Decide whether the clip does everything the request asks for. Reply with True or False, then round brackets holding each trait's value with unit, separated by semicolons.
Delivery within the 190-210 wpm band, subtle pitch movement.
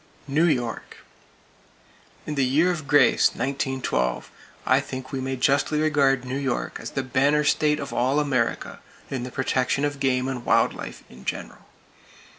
False (160 wpm; 2.3 semitones)